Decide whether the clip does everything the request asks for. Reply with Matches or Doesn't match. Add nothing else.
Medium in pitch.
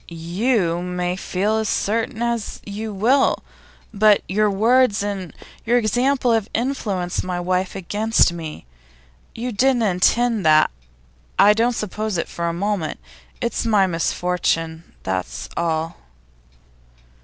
Doesn't match